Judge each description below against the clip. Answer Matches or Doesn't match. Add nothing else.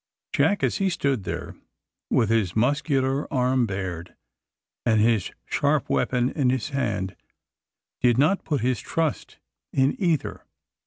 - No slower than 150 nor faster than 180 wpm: Doesn't match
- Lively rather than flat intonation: Doesn't match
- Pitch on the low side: Matches